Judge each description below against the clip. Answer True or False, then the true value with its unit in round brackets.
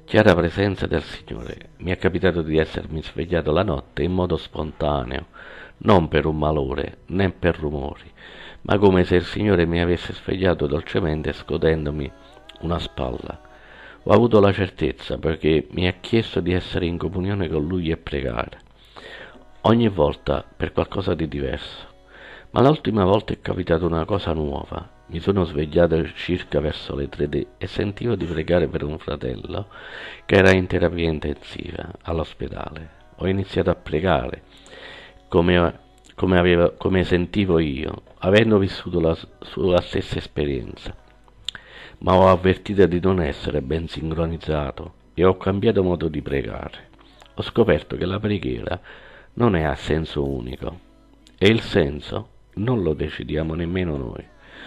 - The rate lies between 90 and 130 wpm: False (145 wpm)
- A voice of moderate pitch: False (85 Hz)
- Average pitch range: True (3.3 semitones)